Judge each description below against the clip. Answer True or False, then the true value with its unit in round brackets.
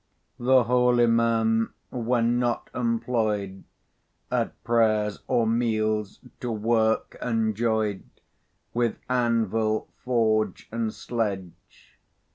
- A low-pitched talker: True (115 Hz)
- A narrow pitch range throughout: True (1.6 semitones)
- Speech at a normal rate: False (85 wpm)